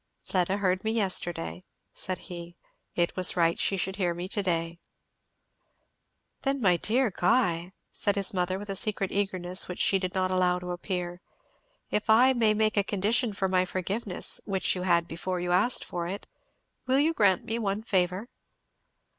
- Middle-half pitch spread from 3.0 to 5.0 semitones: No, narrow, 2.6 semitones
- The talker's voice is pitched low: No, medium, 185 Hz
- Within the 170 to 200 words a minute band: Yes, average, 175 wpm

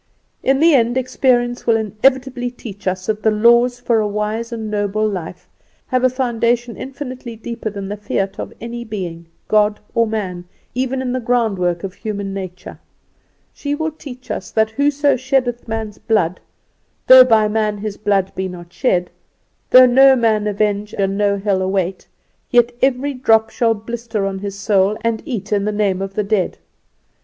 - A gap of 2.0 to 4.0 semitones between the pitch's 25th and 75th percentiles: Yes, average, 3.5 semitones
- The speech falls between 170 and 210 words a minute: Yes, average, 175 wpm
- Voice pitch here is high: Yes, high, 220 Hz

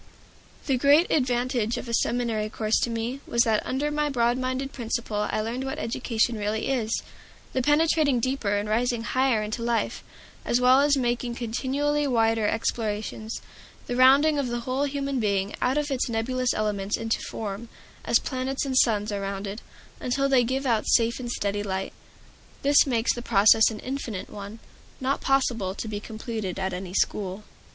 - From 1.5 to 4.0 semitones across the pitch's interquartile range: Yes, average, 3.5 semitones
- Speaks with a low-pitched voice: No, high, 235 Hz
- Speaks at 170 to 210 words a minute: Yes, average, 175 wpm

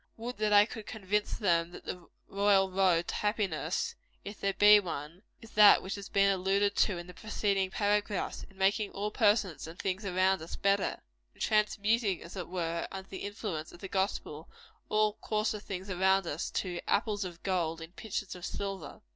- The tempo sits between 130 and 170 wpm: No, average, 190 wpm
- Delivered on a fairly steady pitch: Yes, narrow, 2.3 semitones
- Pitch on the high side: Yes, high, 195 Hz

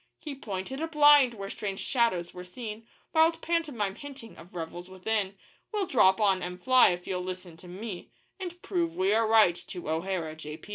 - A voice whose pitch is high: Yes, high, 205 Hz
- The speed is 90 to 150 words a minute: No, average, 180 wpm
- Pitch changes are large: Yes, wide, 6.6 semitones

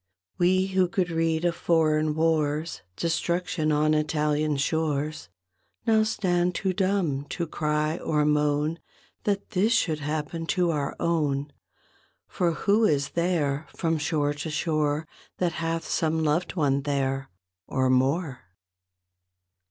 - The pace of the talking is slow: Yes, slow, 130 wpm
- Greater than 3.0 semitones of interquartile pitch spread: No, narrow, 2.6 semitones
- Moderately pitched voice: Yes, medium, 155 Hz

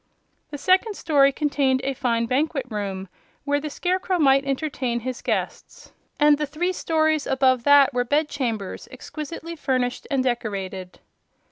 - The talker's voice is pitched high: Yes, very high, 275 Hz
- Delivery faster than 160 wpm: No, average, 145 wpm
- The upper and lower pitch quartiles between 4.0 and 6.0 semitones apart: No, average, 3.6 semitones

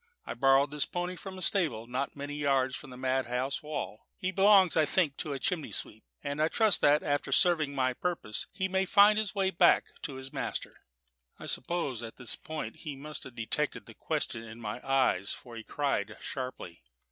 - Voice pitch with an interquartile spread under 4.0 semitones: No, average, 5.3 semitones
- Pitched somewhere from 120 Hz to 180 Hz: Yes, medium, 140 Hz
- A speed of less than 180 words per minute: No, average, 200 wpm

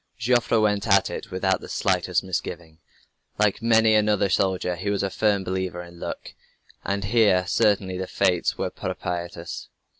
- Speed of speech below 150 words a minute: No, average, 155 wpm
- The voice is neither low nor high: No, very low, 95 Hz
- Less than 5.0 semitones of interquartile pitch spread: Yes, narrow, 2.6 semitones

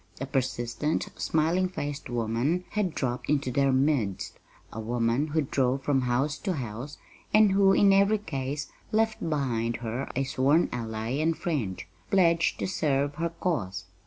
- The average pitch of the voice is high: No, medium, 140 Hz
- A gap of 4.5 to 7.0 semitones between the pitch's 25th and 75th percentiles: Yes, wide, 5.4 semitones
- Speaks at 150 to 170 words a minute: Yes, average, 155 wpm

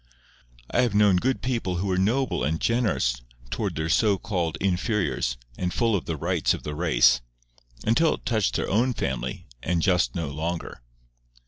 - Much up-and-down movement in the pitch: Yes, wide, 6.3 semitones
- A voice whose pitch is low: Yes, very low, 90 Hz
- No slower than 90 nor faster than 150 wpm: No, average, 165 wpm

